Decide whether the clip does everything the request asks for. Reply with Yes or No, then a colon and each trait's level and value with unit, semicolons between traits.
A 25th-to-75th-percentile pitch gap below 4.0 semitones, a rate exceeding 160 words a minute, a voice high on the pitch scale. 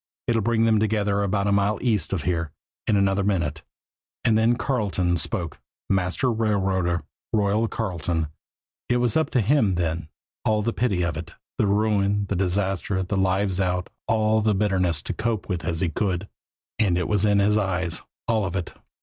No: average, 3.2 semitones; average, 180 wpm; low, 100 Hz